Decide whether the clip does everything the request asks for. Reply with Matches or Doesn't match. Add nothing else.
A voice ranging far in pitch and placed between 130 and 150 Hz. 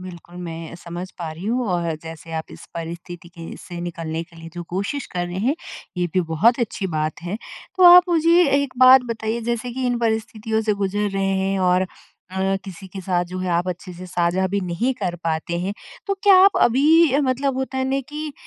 Doesn't match